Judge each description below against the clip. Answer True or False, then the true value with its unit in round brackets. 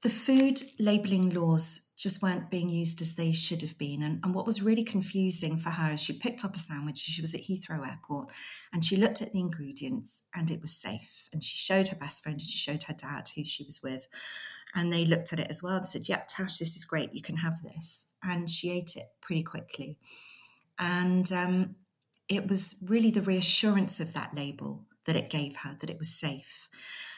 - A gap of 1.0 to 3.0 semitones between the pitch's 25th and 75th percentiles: False (3.5 semitones)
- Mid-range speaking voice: True (170 Hz)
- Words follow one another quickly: True (220 wpm)